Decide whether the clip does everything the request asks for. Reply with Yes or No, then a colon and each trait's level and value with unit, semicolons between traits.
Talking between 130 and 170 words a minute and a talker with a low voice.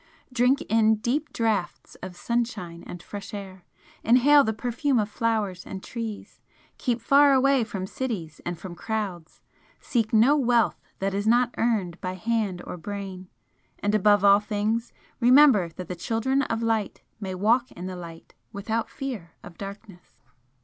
No: average, 155 wpm; high, 215 Hz